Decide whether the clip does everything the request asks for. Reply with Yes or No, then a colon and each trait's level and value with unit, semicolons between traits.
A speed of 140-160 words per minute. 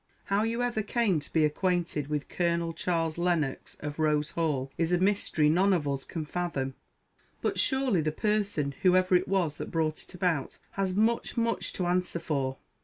No: average, 180 wpm